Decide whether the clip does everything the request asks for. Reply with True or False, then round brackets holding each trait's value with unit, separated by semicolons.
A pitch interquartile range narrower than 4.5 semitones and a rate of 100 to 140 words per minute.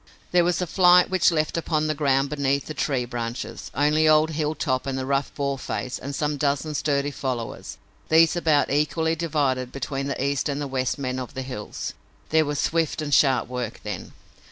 False (2.7 semitones; 190 wpm)